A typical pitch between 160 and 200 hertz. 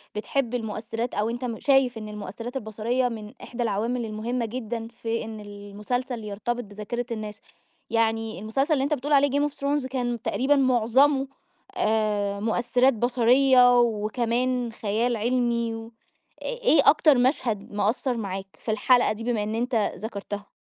No: high, 235 Hz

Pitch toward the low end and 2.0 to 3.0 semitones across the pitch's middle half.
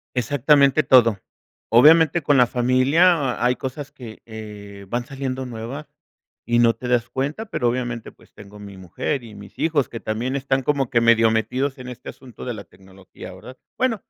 No: low, 125 Hz; average, 3.4 semitones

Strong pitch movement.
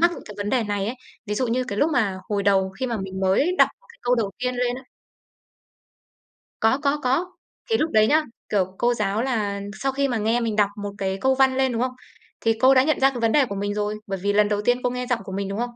No: average, 4.2 semitones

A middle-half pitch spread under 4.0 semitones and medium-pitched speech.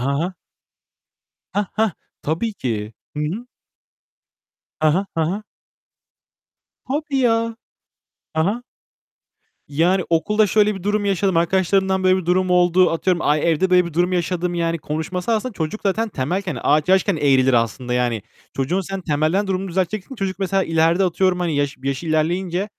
Yes: average, 3.6 semitones; medium, 180 Hz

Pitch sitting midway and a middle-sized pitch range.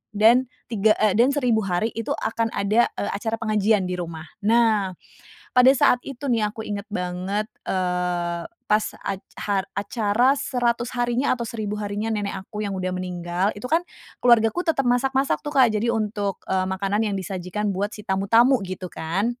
No: high, 210 Hz; average, 3.6 semitones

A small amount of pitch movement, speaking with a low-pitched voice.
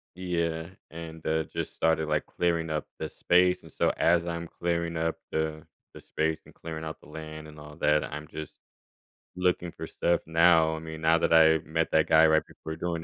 Yes: narrow, 1.1 semitones; very low, 80 Hz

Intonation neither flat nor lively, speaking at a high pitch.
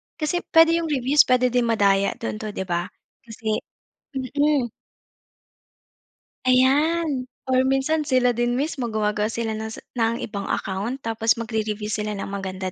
Yes: average, 3.9 semitones; high, 235 Hz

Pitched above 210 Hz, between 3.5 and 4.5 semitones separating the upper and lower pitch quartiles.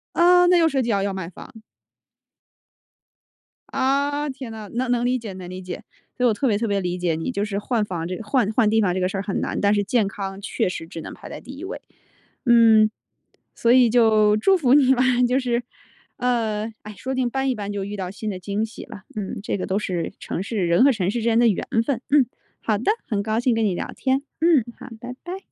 Yes: high, 220 Hz; average, 4.2 semitones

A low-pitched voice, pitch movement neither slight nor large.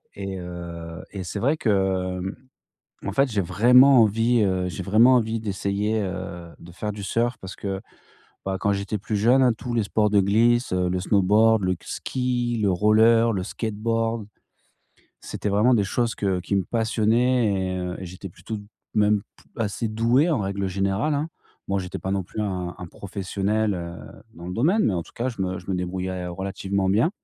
Yes: low, 100 Hz; average, 3.4 semitones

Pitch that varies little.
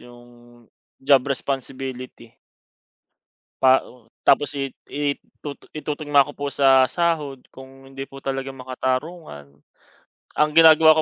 Yes: narrow, 2.2 semitones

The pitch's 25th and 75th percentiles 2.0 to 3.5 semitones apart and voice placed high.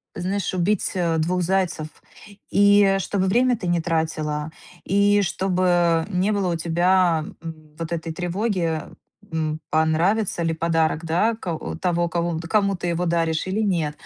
No: average, 2.9 semitones; medium, 175 Hz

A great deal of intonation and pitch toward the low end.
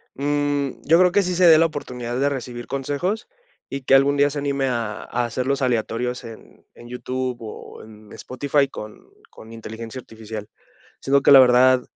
No: average, 3.1 semitones; low, 130 Hz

